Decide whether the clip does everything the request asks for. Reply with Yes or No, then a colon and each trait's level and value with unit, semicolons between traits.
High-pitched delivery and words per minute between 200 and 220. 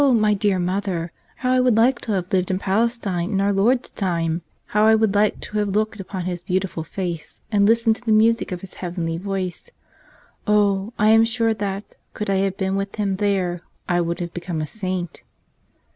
Yes: high, 195 Hz; fast, 205 wpm